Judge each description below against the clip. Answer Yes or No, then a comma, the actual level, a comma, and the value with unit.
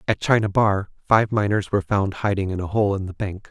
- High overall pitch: No, low, 100 Hz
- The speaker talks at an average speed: No, fast, 240 wpm